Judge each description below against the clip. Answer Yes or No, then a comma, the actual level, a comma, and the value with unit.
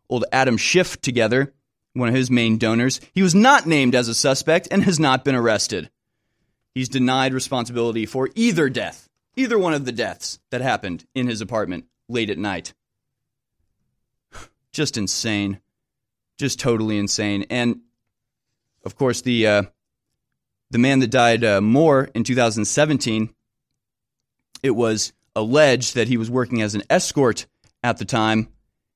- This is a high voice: No, low, 120 Hz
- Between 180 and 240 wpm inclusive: No, average, 145 wpm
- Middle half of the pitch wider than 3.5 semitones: No, average, 3.0 semitones